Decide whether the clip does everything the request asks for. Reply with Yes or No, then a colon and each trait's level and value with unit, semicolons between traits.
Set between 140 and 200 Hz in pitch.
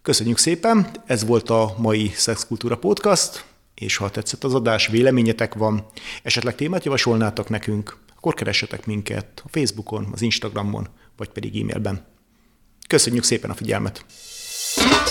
No: low, 110 Hz